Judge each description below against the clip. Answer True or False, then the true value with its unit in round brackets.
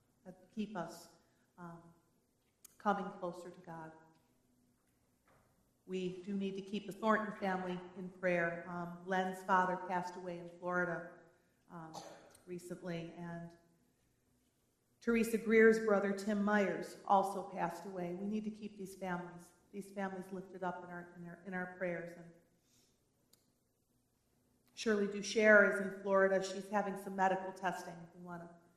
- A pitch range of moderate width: False (2.3 semitones)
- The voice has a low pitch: False (180 Hz)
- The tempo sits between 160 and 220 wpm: False (140 wpm)